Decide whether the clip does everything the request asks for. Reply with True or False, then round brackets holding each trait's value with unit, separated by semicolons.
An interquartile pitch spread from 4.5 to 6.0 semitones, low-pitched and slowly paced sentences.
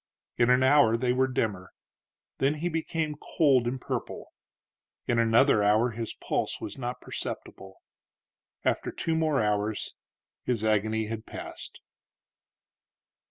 False (3.8 semitones; 120 Hz; 125 wpm)